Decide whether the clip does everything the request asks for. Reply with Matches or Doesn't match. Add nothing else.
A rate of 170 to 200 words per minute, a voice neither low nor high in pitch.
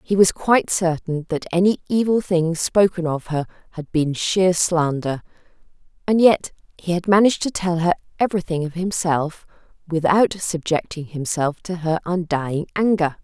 Doesn't match